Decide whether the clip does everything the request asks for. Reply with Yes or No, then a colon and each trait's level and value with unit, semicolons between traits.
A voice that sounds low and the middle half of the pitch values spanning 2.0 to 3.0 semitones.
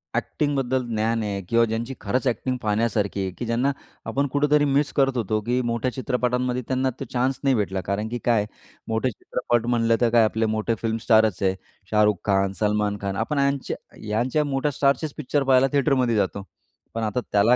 No: low, 120 Hz; average, 3.7 semitones